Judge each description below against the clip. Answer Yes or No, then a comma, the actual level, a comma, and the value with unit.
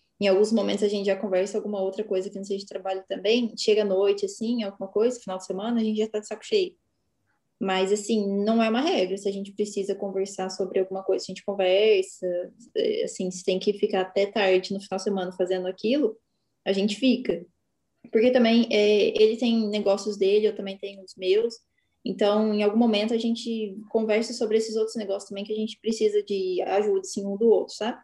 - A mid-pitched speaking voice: No, high, 205 Hz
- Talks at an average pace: No, fast, 215 wpm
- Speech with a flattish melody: Yes, narrow, 2.2 semitones